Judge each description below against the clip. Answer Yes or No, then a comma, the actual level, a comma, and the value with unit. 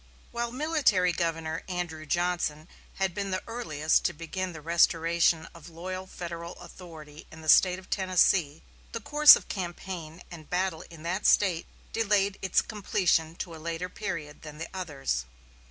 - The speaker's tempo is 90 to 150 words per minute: No, average, 160 wpm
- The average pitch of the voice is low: No, medium, 175 Hz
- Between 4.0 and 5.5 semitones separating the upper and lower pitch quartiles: No, average, 2.7 semitones